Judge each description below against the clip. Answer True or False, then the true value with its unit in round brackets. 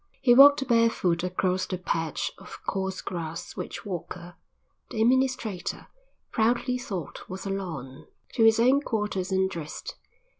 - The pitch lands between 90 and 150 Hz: False (190 Hz)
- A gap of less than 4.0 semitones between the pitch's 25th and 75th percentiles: False (4.8 semitones)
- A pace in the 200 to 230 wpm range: False (140 wpm)